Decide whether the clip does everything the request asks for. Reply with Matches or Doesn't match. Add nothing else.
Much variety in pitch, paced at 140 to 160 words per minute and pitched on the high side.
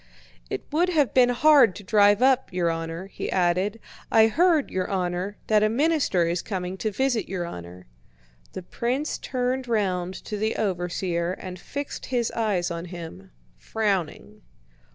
Matches